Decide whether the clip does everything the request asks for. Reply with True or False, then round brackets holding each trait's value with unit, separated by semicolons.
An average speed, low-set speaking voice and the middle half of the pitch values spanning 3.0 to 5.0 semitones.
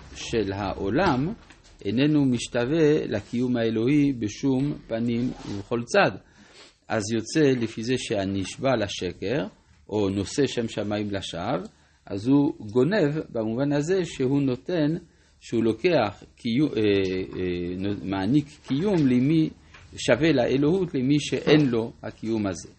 False (115 wpm; 120 Hz; 5.4 semitones)